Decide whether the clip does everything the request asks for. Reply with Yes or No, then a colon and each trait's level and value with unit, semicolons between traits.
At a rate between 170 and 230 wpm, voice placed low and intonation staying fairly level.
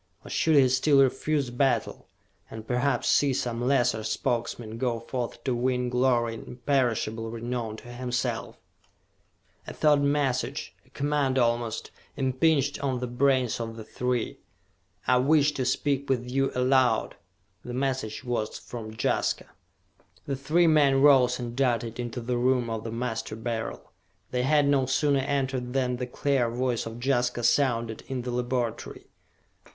No: average, 150 wpm; low, 125 Hz; narrow, 2.3 semitones